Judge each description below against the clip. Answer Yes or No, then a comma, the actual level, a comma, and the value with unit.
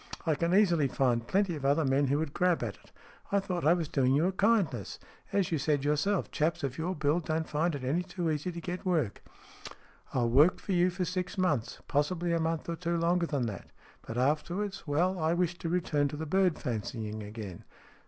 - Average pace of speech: No, fast, 220 wpm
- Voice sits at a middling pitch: Yes, medium, 160 Hz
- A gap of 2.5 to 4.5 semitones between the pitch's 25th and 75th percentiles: Yes, average, 4.1 semitones